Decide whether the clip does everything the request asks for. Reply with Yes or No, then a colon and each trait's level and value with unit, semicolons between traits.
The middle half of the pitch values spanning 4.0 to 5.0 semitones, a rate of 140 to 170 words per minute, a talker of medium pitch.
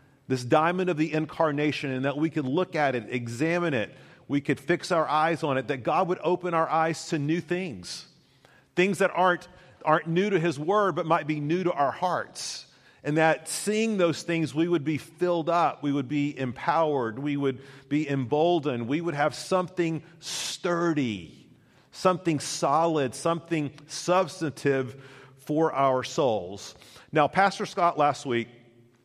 No: average, 3.5 semitones; average, 165 wpm; medium, 155 Hz